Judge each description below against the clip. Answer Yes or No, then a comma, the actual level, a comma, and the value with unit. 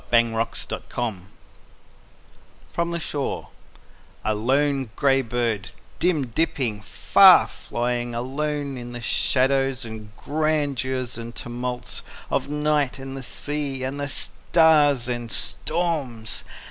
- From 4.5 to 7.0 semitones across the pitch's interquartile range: No, average, 3.4 semitones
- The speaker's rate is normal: No, slow, 120 wpm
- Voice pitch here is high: No, low, 130 Hz